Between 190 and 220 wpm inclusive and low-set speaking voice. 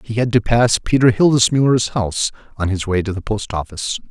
Yes: fast, 205 wpm; low, 110 Hz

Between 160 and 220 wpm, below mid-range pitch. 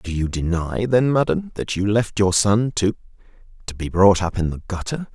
Yes: average, 200 wpm; low, 100 Hz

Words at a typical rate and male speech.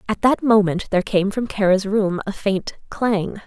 No: average, 190 wpm; female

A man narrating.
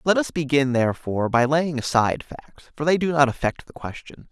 Yes: male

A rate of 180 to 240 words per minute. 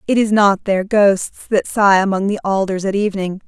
Yes: fast, 205 wpm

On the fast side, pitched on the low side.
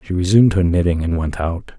Yes: fast, 235 wpm; very low, 90 Hz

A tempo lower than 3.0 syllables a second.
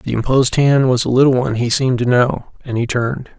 No: 6.1 syllables/s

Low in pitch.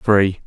Yes: low, 100 Hz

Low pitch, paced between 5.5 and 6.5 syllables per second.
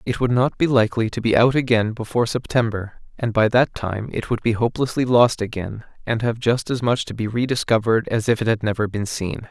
Yes: low, 115 Hz; 5.8 syllables/s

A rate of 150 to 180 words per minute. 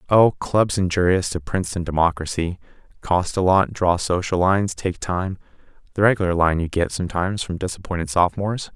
Yes: average, 160 wpm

